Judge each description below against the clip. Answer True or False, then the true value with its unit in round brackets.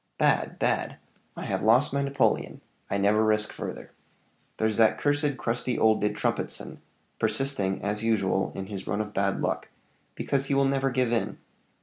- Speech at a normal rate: True (165 wpm)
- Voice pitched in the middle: False (110 Hz)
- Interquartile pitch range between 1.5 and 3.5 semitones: False (4.6 semitones)